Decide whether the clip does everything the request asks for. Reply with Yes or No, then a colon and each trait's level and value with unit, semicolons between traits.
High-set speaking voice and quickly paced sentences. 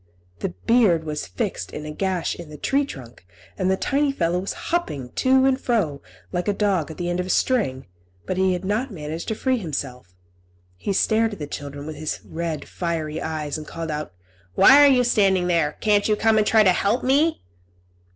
No: medium, 180 Hz; fast, 210 wpm